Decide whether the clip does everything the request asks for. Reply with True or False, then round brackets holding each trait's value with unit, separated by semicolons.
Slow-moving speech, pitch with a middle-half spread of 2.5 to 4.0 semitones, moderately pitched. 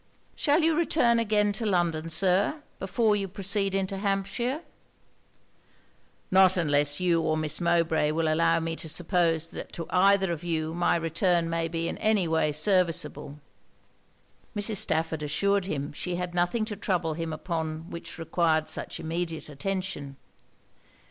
False (150 wpm; 3.4 semitones; 175 Hz)